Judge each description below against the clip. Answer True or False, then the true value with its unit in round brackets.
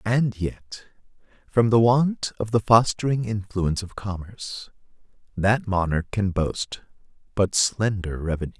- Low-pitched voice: True (105 Hz)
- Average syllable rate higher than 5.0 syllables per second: False (4.3 syllables/s)